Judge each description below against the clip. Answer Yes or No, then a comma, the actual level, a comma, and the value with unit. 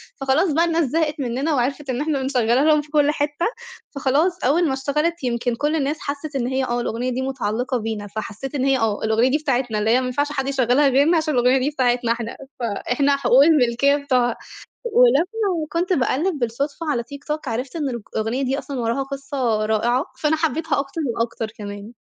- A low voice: No, very high, 270 Hz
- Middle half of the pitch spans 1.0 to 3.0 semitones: No, average, 3.7 semitones